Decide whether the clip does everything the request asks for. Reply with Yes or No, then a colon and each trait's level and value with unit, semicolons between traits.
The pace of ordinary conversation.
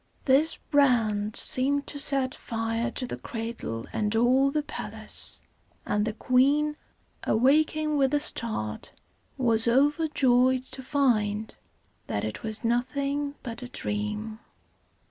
No: slow, 125 wpm